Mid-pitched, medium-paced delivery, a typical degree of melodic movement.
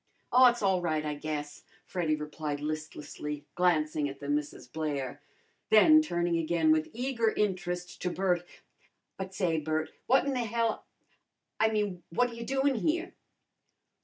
No: medium, 175 Hz; average, 160 wpm; wide, 6.2 semitones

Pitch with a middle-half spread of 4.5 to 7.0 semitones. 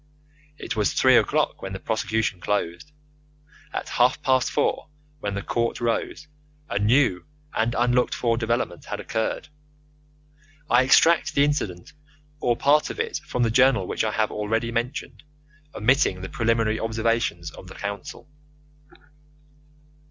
No: average, 3.2 semitones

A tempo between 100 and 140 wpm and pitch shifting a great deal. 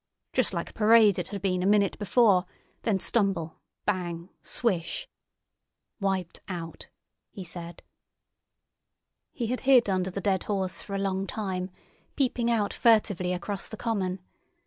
No: slow, 135 wpm; average, 2.9 semitones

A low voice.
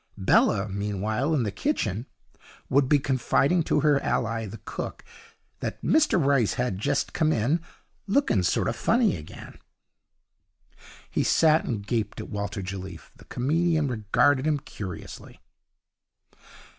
Yes: low, 125 Hz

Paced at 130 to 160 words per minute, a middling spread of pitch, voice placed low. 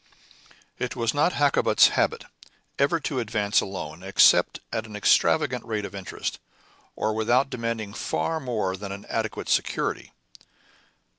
Yes: average, 140 wpm; average, 4.1 semitones; low, 110 Hz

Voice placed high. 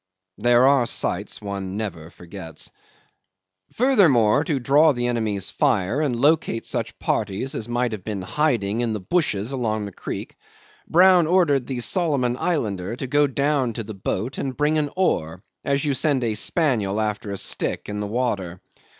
No: low, 120 Hz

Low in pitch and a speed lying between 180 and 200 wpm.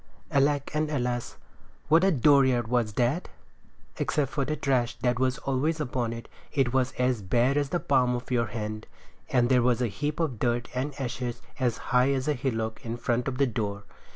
Yes: low, 125 Hz; average, 195 wpm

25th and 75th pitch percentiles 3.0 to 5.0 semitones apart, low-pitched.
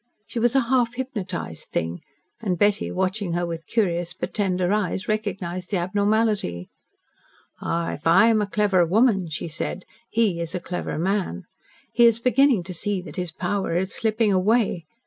No: average, 3.9 semitones; high, 190 Hz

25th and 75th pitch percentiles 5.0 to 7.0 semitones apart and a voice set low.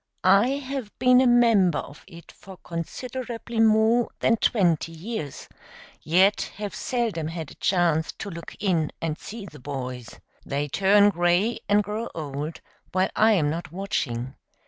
No: wide, 5.6 semitones; high, 190 Hz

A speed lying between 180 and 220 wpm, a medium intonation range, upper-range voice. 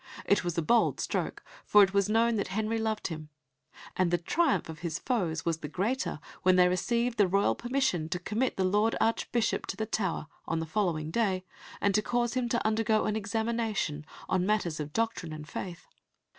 Yes: average, 200 wpm; average, 4.7 semitones; high, 200 Hz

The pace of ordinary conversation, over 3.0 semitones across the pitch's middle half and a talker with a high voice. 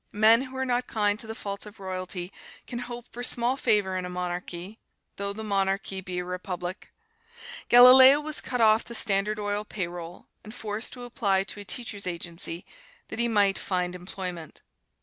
Yes: average, 180 wpm; average, 4.2 semitones; high, 205 Hz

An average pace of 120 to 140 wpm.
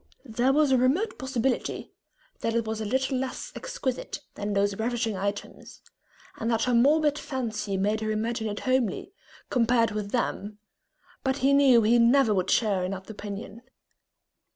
No: average, 160 wpm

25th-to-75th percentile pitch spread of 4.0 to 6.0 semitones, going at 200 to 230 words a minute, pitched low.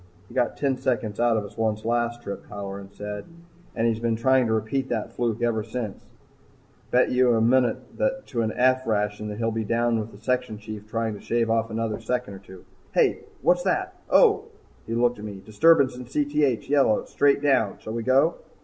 No: average, 3.0 semitones; fast, 205 wpm; low, 115 Hz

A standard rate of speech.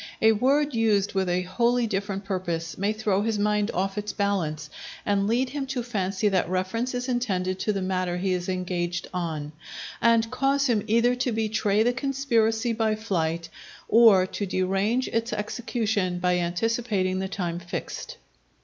Yes: average, 165 wpm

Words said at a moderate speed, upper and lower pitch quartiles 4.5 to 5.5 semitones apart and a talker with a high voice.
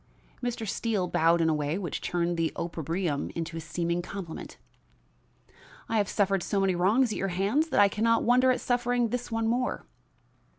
Yes: average, 185 wpm; average, 5.1 semitones; high, 195 Hz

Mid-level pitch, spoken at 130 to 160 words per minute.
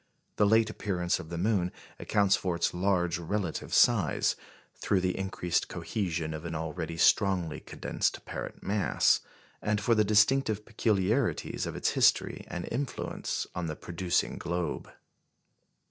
No: very low, 95 Hz; average, 140 wpm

